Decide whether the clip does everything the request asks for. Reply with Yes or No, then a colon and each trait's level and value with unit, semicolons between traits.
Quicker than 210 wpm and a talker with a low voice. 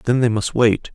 Yes: fast, 255 wpm; low, 115 Hz